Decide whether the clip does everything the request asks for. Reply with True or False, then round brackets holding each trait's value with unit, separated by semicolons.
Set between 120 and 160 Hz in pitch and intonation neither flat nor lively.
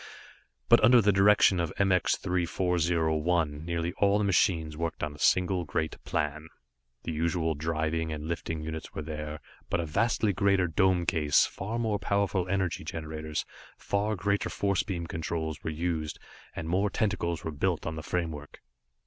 False (85 Hz; 3.3 semitones)